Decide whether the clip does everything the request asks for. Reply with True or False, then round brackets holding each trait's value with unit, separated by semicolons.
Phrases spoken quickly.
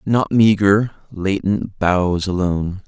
False (105 wpm)